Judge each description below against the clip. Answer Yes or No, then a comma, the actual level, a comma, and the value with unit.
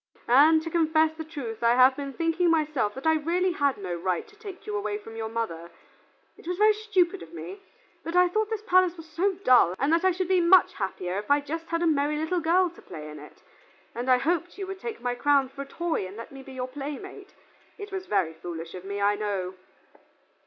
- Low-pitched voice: No, very high, 290 Hz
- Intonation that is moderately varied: No, wide, 8.5 semitones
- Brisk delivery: Yes, fast, 235 wpm